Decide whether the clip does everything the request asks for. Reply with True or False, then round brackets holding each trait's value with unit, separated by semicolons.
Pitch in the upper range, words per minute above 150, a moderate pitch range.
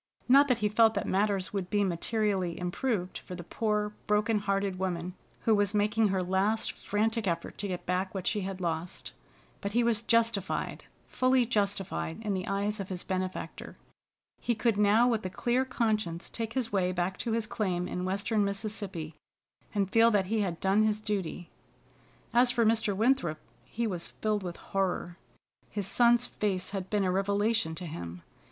True (205 Hz; 180 wpm; 3.1 semitones)